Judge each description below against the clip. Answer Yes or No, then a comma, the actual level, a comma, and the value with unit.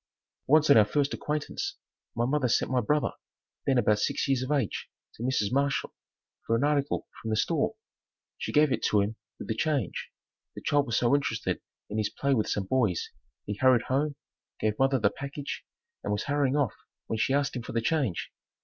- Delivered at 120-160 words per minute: No, average, 200 wpm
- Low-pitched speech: Yes, low, 130 Hz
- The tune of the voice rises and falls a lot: No, average, 4.4 semitones